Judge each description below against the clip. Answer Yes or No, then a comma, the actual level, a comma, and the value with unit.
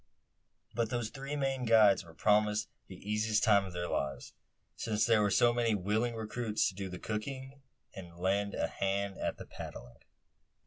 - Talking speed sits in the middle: Yes, average, 175 wpm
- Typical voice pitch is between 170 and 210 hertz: No, low, 105 Hz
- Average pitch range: Yes, average, 3.1 semitones